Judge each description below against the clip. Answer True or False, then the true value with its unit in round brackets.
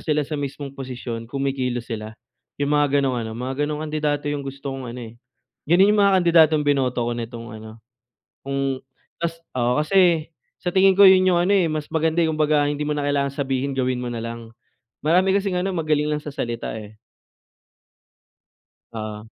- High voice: False (145 Hz)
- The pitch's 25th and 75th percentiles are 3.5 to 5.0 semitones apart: True (4.2 semitones)